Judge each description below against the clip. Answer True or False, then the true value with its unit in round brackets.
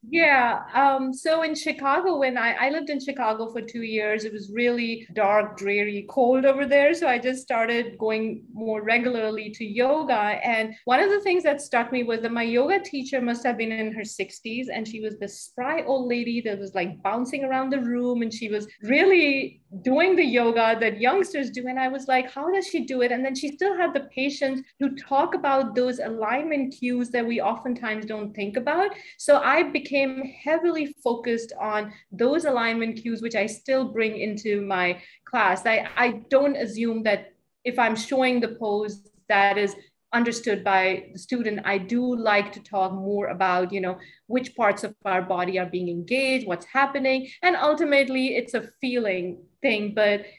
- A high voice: True (235 Hz)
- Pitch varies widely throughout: False (4.2 semitones)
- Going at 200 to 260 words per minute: False (190 wpm)